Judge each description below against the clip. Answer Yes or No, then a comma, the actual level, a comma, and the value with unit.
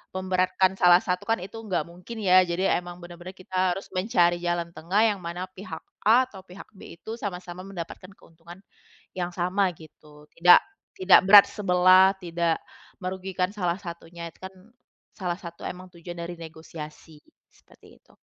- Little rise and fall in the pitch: Yes, narrow, 1.6 semitones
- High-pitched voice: No, medium, 180 Hz